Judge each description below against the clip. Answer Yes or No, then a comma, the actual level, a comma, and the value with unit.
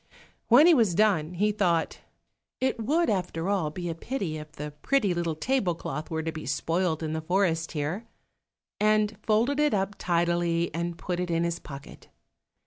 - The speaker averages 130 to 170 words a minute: No, average, 180 wpm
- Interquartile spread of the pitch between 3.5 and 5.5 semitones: Yes, average, 4.5 semitones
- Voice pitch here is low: No, medium, 175 Hz